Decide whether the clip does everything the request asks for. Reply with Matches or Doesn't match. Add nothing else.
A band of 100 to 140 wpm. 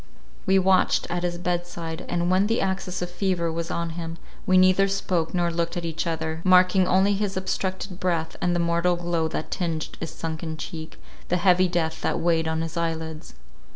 Doesn't match